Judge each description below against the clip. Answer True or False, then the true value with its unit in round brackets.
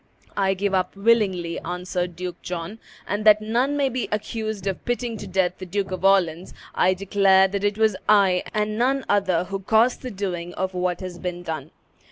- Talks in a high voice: True (195 Hz)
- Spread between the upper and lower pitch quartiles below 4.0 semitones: True (2.9 semitones)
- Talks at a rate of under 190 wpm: False (195 wpm)